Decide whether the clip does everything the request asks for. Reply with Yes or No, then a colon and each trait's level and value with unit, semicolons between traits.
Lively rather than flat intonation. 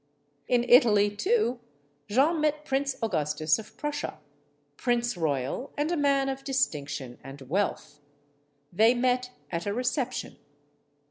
Yes: wide, 8.3 semitones